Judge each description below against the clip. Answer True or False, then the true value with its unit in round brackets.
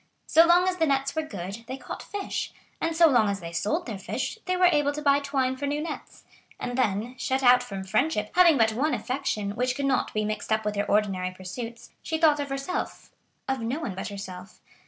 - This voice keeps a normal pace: False (220 wpm)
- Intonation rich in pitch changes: True (6.1 semitones)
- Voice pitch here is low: False (255 Hz)